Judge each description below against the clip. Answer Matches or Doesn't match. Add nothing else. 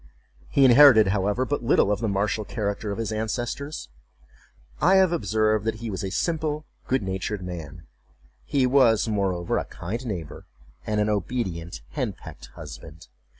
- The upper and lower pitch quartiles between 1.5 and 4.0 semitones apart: Doesn't match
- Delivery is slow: Doesn't match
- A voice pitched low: Matches